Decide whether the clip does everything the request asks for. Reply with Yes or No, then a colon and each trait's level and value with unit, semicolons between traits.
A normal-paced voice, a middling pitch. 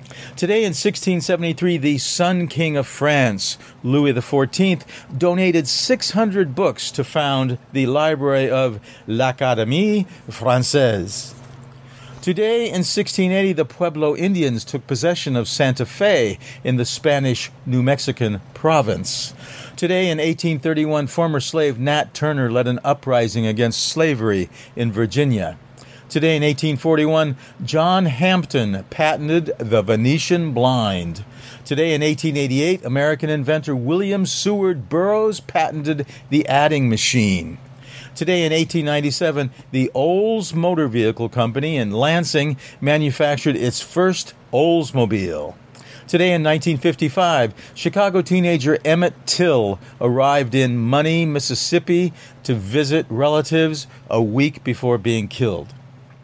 No: slow, 110 wpm; medium, 145 Hz